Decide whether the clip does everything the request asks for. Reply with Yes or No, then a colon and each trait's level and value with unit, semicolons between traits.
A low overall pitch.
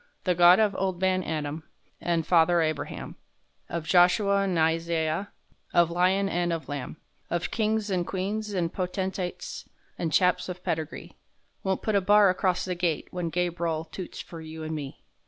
No: medium, 175 Hz